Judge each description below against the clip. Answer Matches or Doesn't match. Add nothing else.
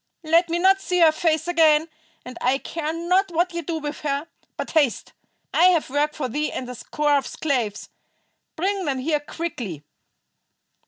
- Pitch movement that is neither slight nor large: Matches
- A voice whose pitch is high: Matches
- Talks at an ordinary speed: Matches